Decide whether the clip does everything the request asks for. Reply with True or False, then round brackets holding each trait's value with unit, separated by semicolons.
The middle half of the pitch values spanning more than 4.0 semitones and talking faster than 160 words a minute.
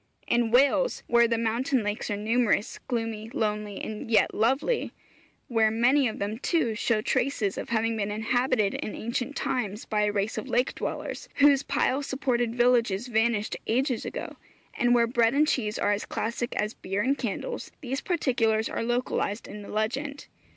False (3.0 semitones; 170 wpm)